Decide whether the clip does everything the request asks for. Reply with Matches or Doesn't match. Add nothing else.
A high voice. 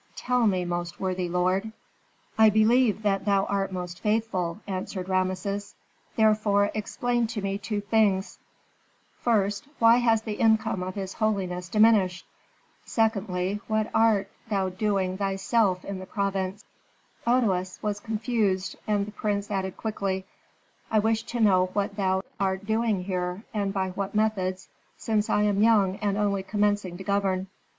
Matches